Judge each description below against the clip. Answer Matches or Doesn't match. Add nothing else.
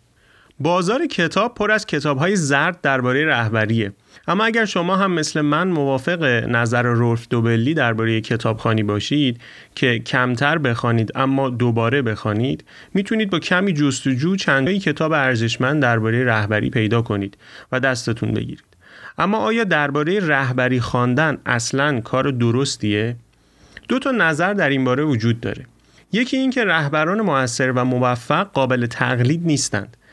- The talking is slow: Doesn't match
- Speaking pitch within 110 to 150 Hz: Matches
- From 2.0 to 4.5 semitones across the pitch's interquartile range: Doesn't match